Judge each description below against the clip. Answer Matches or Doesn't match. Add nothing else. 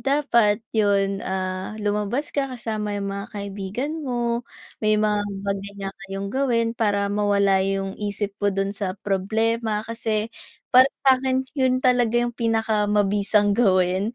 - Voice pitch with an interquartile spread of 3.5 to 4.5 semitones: Doesn't match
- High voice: Matches